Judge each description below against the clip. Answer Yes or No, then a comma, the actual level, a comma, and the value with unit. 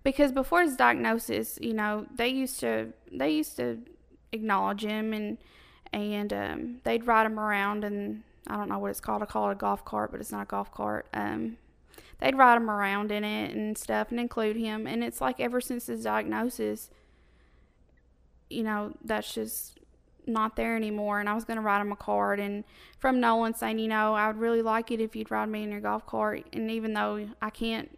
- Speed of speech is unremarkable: No, fast, 215 wpm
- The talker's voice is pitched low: No, high, 200 Hz